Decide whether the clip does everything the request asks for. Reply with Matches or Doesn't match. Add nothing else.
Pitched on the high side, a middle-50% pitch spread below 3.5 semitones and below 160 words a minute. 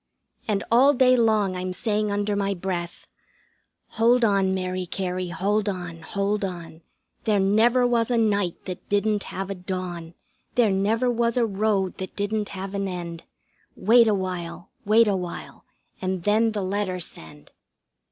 Matches